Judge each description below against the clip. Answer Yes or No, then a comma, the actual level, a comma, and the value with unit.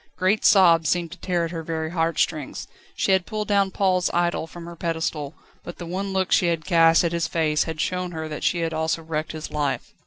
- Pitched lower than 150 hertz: No, medium, 170 Hz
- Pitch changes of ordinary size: No, narrow, 2.2 semitones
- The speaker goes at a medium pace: No, fast, 235 wpm